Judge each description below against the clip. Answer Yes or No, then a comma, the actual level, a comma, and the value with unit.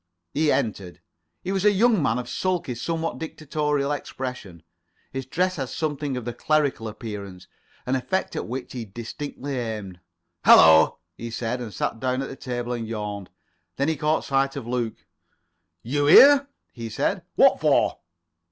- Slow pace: No, average, 160 wpm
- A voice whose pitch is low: Yes, low, 130 Hz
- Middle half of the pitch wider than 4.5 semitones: Yes, average, 4.9 semitones